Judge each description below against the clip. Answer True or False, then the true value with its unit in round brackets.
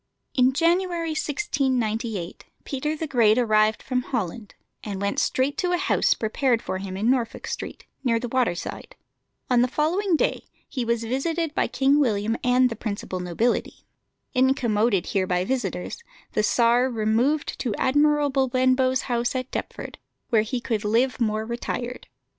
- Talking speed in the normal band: True (155 wpm)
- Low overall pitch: False (245 Hz)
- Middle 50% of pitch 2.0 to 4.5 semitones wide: True (3.6 semitones)